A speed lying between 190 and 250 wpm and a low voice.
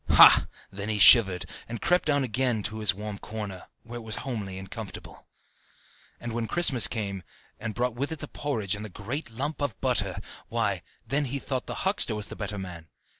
Yes: average, 195 wpm; low, 110 Hz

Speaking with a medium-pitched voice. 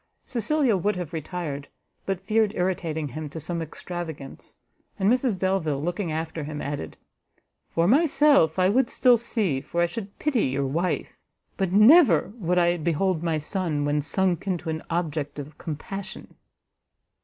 Yes: medium, 175 Hz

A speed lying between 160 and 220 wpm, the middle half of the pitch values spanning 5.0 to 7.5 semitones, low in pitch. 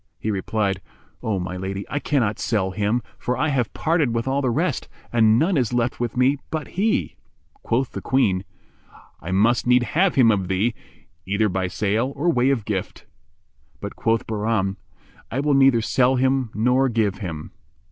No: average, 180 wpm; average, 4.6 semitones; low, 115 Hz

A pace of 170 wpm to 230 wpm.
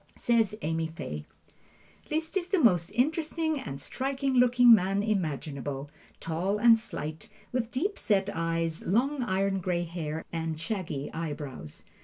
No: slow, 135 wpm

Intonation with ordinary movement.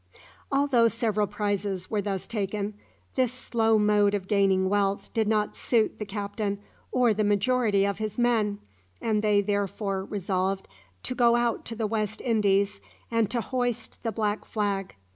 No: narrow, 2.3 semitones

